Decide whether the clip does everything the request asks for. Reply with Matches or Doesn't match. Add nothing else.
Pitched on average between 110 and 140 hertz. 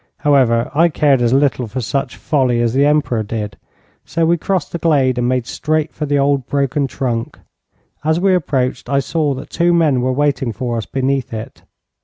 Matches